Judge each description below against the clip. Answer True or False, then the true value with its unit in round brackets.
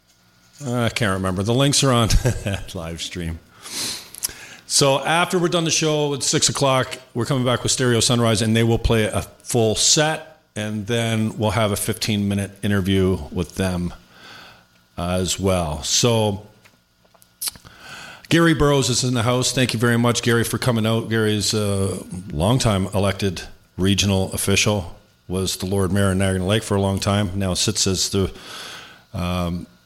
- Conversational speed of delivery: True (160 wpm)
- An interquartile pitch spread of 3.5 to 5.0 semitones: True (4.2 semitones)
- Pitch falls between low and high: False (105 Hz)